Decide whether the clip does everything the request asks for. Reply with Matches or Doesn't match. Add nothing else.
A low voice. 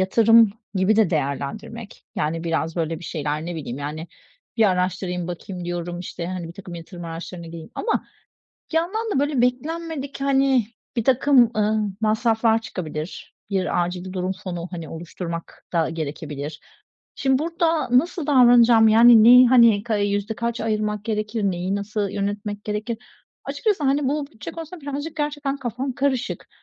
Doesn't match